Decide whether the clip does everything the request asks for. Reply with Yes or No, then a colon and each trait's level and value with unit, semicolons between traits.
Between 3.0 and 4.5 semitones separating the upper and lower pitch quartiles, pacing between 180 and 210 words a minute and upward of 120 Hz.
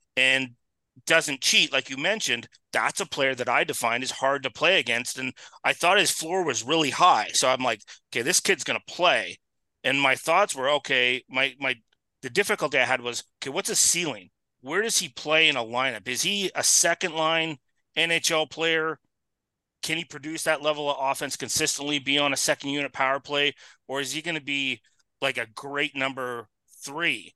Yes: average, 3.4 semitones; average, 195 wpm; medium, 140 Hz